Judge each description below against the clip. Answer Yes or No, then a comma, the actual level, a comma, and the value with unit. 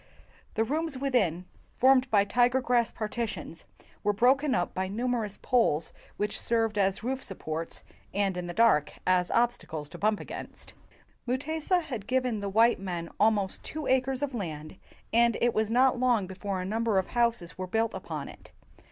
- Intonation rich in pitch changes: No, average, 4.7 semitones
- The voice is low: No, high, 225 Hz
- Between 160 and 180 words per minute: Yes, average, 170 wpm